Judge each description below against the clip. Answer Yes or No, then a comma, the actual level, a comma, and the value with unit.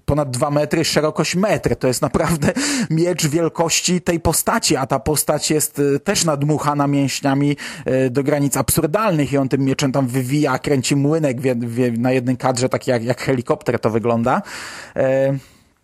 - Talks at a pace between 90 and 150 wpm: No, fast, 160 wpm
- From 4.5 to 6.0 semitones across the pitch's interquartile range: No, average, 3.4 semitones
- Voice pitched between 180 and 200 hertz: No, medium, 145 Hz